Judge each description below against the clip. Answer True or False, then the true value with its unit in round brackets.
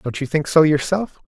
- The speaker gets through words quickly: True (235 wpm)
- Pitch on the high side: False (155 Hz)